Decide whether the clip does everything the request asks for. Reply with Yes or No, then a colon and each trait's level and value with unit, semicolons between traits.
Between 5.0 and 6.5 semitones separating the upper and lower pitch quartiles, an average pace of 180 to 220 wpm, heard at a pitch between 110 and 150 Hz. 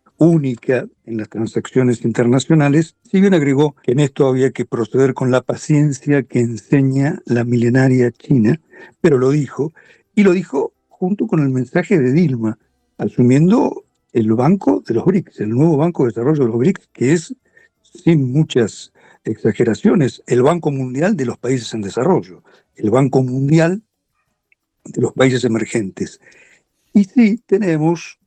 No: wide, 5.6 semitones; average, 150 wpm; medium, 140 Hz